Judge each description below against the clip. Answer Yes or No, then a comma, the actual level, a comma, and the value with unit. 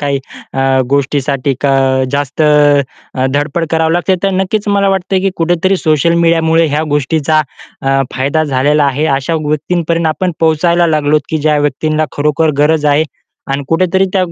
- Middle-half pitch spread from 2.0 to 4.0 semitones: Yes, average, 2.7 semitones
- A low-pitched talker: No, medium, 155 Hz